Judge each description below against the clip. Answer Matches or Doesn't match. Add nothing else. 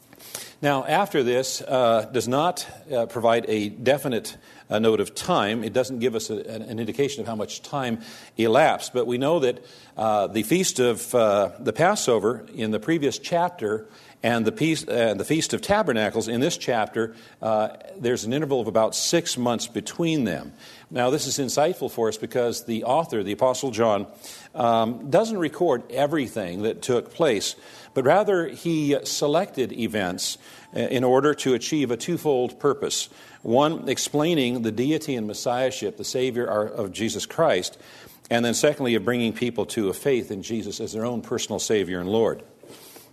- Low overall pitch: Matches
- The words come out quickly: Doesn't match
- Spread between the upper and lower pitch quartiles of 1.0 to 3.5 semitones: Doesn't match